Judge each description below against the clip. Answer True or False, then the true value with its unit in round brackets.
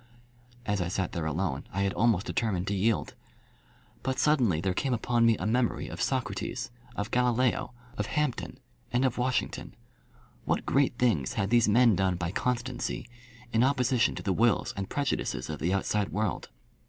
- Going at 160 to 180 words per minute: True (170 wpm)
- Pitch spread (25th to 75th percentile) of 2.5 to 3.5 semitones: False (4.4 semitones)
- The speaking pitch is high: False (115 Hz)